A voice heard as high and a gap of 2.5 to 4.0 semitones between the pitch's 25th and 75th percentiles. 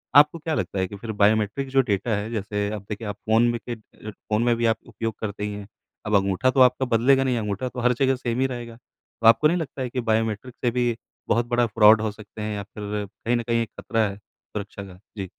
No: low, 115 Hz; average, 2.9 semitones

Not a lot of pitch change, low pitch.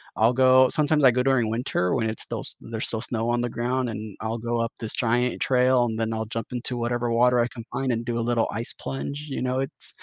Yes: narrow, 1.9 semitones; low, 120 Hz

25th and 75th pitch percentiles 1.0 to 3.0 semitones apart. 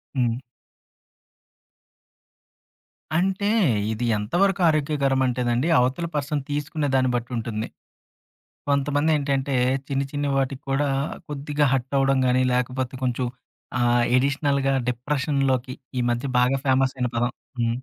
Yes: narrow, 2.6 semitones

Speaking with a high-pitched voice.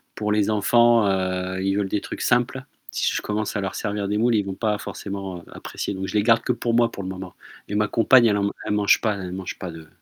No: low, 105 Hz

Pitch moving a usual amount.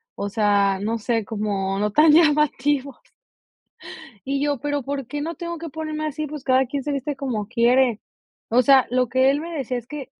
Yes: average, 4.1 semitones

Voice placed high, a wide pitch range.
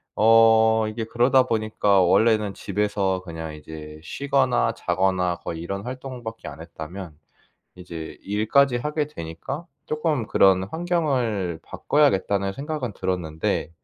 No: low, 105 Hz; wide, 5.8 semitones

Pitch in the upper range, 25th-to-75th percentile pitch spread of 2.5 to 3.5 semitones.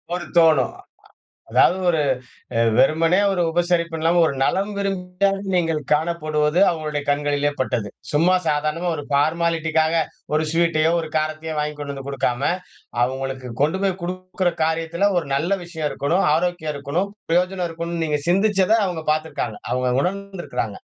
No: medium, 160 Hz; average, 3.1 semitones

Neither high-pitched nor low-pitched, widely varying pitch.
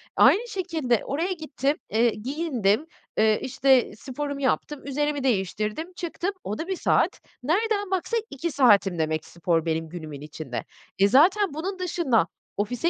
No: very high, 275 Hz; wide, 8.3 semitones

